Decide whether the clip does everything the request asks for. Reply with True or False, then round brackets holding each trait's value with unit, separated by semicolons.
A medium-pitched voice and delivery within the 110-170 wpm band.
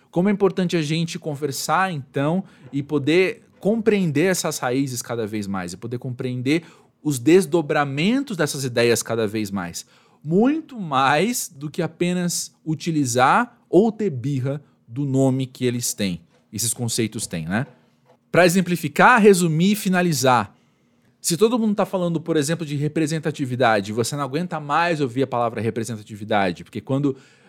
True (150 Hz; 145 wpm)